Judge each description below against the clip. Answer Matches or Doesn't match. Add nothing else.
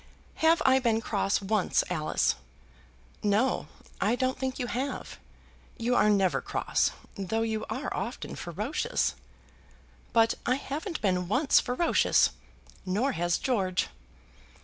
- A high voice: Matches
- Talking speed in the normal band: Doesn't match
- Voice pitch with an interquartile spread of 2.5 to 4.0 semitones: Doesn't match